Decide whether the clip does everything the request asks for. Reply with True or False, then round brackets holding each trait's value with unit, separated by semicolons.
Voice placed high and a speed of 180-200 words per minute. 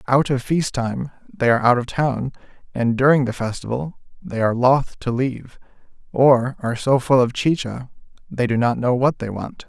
False (125 Hz; 190 wpm)